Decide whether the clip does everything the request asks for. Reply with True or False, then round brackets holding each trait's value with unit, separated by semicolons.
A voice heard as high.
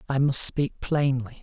False (135 Hz)